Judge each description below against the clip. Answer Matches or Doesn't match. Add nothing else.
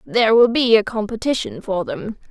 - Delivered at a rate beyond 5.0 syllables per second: Matches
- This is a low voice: Doesn't match